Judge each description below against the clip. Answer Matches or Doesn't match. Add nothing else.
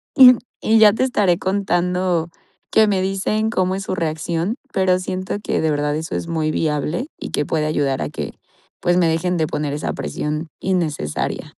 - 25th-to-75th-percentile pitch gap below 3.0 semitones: Doesn't match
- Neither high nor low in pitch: Matches